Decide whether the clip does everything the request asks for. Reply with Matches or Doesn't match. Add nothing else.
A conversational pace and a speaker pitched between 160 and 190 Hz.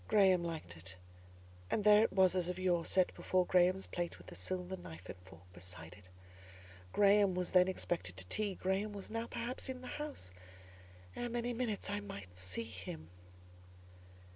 Matches